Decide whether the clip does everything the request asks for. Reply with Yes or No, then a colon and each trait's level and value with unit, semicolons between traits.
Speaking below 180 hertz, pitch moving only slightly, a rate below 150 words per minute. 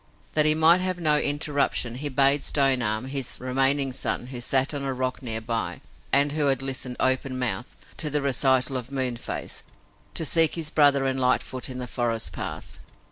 No: low, 135 Hz; narrow, 2.3 semitones; average, 190 wpm